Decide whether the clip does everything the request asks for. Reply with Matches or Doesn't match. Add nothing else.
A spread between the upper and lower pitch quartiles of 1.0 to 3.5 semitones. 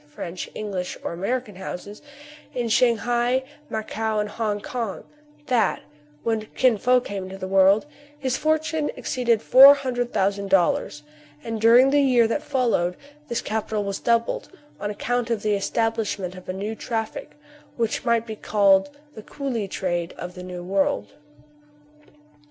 Doesn't match